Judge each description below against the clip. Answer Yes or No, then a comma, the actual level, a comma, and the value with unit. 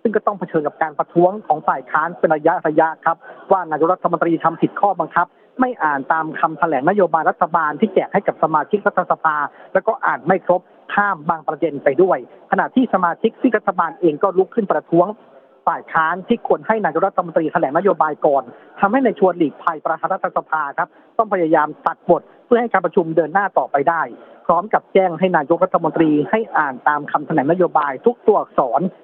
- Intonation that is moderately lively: Yes, average, 3.5 semitones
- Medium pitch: Yes, medium, 175 Hz